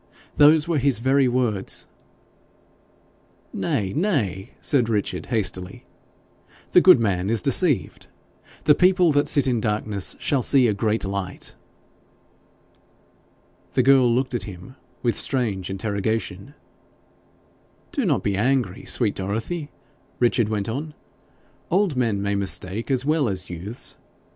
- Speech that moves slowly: Yes, slow, 125 wpm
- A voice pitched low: Yes, low, 115 Hz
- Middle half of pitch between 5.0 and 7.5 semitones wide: Yes, wide, 5.6 semitones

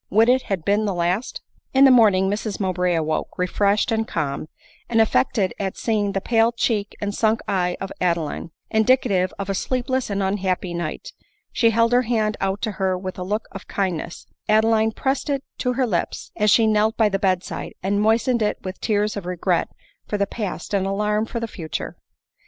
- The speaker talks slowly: No, average, 200 wpm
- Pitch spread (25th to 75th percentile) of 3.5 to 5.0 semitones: No, average, 3.1 semitones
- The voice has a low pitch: No, high, 205 Hz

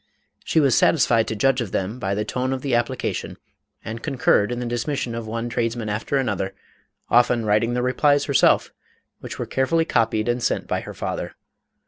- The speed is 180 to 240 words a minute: Yes, average, 185 wpm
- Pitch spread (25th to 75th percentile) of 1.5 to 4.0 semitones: Yes, narrow, 2.6 semitones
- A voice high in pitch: No, low, 120 Hz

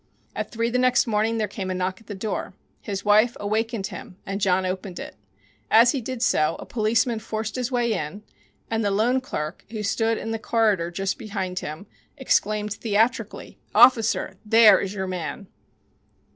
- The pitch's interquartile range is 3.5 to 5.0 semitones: No, average, 2.9 semitones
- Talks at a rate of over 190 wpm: No, average, 180 wpm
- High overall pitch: Yes, high, 215 Hz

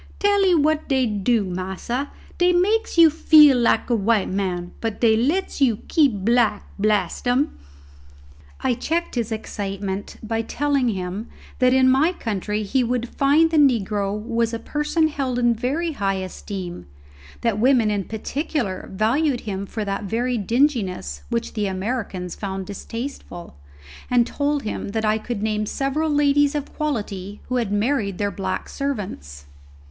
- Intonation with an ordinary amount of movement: No, wide, 5.7 semitones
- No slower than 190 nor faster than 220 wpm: No, average, 160 wpm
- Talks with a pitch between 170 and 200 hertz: No, high, 230 Hz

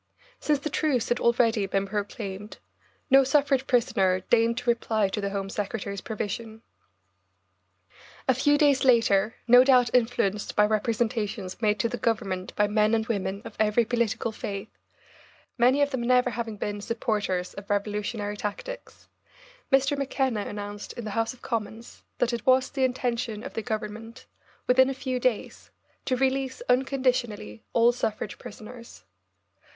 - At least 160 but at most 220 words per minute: No, average, 150 wpm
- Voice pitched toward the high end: Yes, high, 230 Hz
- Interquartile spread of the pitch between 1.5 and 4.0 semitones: Yes, average, 3.4 semitones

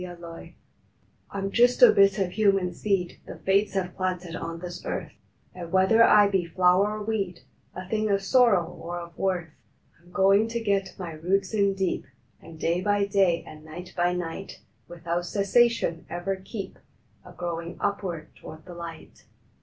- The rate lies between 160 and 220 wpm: Yes, average, 175 wpm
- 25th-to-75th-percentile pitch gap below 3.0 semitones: Yes, narrow, 2.5 semitones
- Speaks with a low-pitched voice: No, medium, 185 Hz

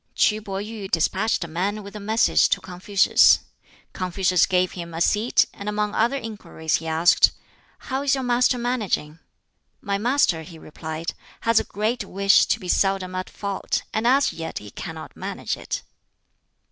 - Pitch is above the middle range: Yes, high, 200 Hz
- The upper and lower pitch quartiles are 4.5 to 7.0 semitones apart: No, average, 3.9 semitones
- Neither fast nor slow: Yes, average, 170 wpm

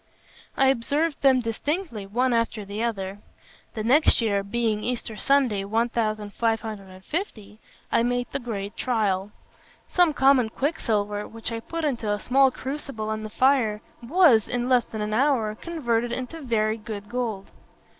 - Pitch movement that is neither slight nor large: Yes, average, 3.7 semitones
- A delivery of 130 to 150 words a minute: Yes, average, 145 wpm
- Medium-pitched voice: No, high, 230 Hz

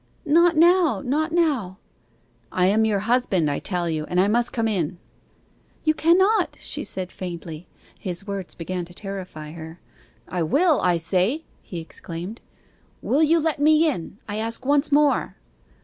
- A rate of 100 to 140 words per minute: No, average, 160 wpm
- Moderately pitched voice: No, high, 205 Hz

